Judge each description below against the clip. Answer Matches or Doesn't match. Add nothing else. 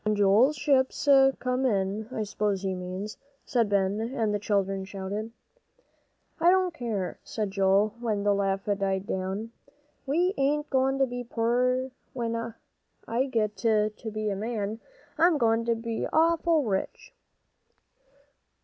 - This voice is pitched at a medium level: Doesn't match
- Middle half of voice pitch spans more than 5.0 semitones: Doesn't match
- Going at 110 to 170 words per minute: Matches